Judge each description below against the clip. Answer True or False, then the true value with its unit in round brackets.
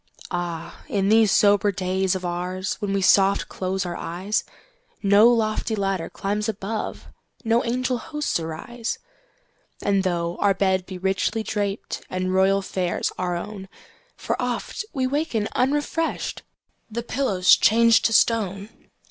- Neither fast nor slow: False (115 wpm)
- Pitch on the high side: True (200 Hz)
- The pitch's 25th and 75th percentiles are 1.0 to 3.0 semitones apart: False (3.5 semitones)